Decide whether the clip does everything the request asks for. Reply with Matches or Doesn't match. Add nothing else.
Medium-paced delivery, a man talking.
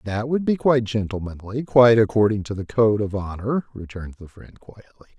Matches